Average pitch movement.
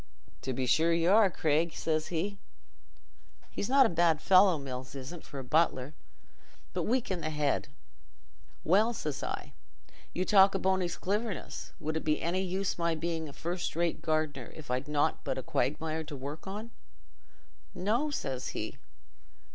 Yes: average, 4.1 semitones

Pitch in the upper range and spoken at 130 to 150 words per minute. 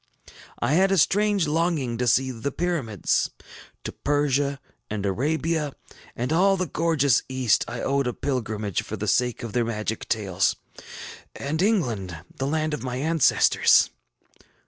No: low, 135 Hz; average, 145 wpm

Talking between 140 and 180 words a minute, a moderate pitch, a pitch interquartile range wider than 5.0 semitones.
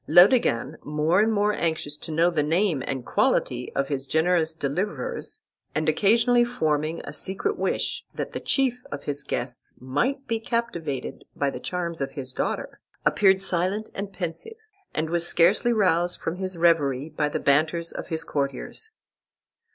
Yes: average, 160 wpm; medium, 170 Hz; wide, 5.6 semitones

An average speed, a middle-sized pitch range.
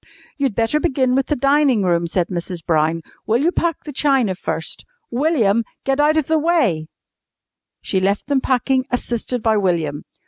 No: average, 170 wpm; wide, 7.1 semitones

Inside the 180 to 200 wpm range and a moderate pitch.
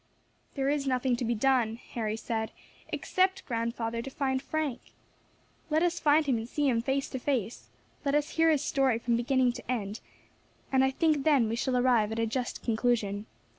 No: average, 190 wpm; very high, 255 Hz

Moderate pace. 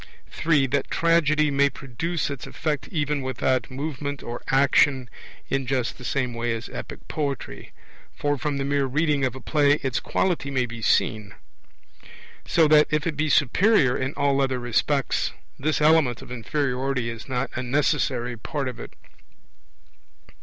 Yes: average, 160 wpm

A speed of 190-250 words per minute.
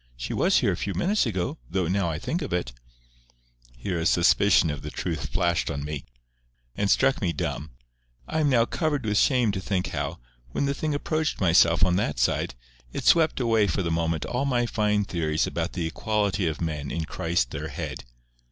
Yes: average, 200 wpm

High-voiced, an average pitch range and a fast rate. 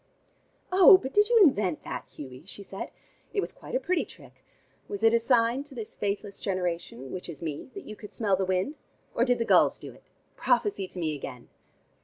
No: high, 210 Hz; wide, 7.3 semitones; fast, 210 wpm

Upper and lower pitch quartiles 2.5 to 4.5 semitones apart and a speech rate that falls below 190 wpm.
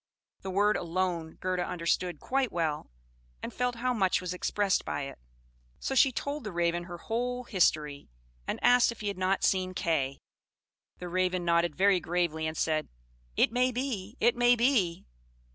No: wide, 5.6 semitones; average, 170 wpm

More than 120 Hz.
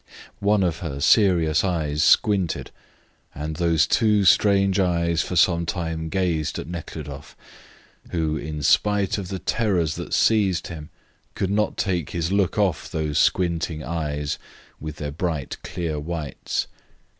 No: very low, 85 Hz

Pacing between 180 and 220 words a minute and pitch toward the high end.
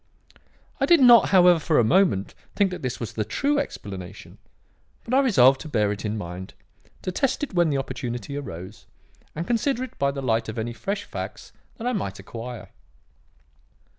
No: average, 185 wpm; medium, 140 Hz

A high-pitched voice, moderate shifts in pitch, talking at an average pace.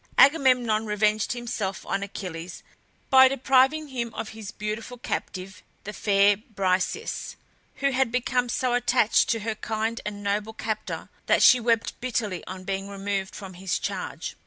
Yes: high, 220 Hz; average, 3.7 semitones; average, 150 wpm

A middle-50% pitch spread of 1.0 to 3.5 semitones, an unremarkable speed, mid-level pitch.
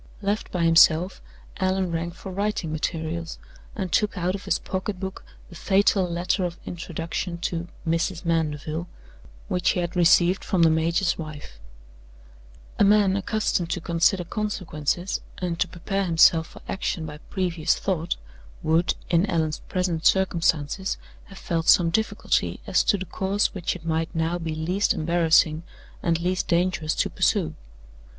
Yes: narrow, 2.4 semitones; average, 150 wpm; medium, 175 Hz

